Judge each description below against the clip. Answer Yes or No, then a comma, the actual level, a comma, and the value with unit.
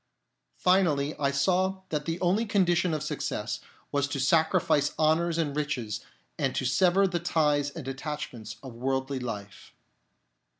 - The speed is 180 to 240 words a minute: No, average, 140 wpm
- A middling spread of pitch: Yes, average, 4.3 semitones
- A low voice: No, medium, 150 Hz